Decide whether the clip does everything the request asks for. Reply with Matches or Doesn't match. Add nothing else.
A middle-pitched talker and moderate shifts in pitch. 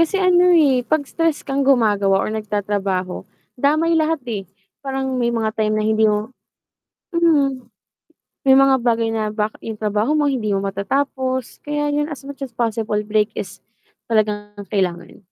Doesn't match